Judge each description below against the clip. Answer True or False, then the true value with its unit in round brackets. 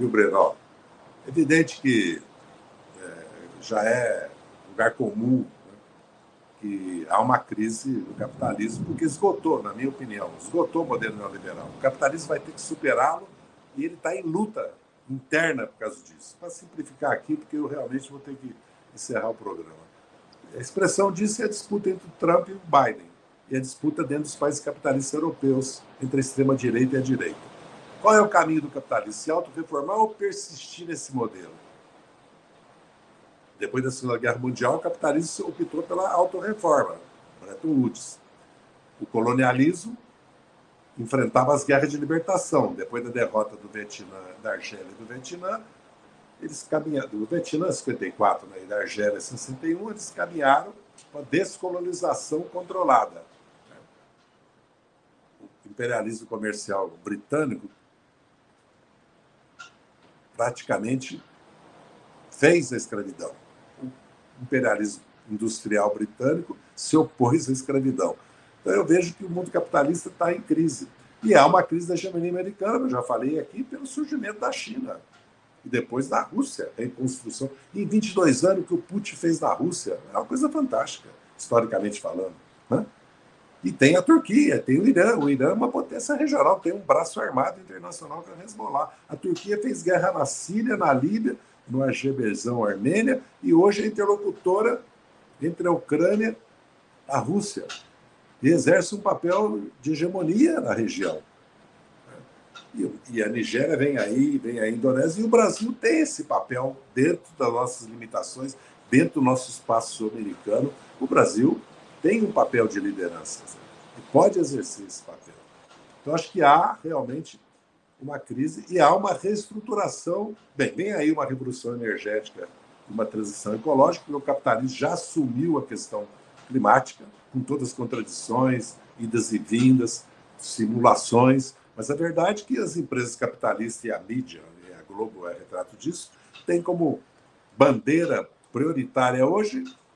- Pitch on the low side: False (155 Hz)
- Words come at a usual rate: True (150 wpm)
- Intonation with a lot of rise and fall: True (7.7 semitones)